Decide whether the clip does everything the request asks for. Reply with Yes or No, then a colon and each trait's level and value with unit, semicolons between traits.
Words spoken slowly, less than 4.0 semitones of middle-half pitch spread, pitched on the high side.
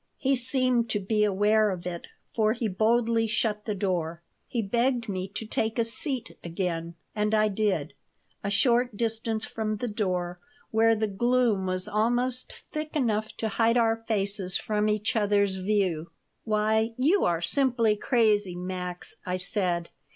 No: average, 160 wpm; average, 3.2 semitones; high, 215 Hz